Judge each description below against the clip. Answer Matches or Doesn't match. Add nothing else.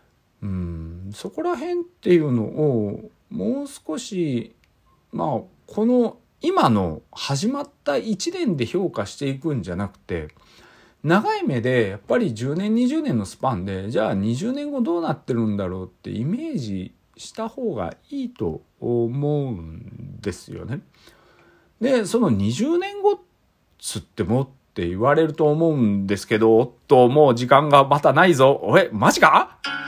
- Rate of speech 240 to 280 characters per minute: Matches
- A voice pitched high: Doesn't match